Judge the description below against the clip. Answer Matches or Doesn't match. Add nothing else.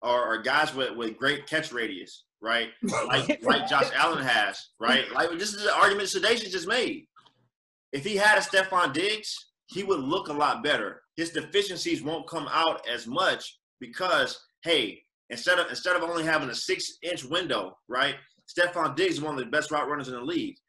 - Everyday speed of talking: Matches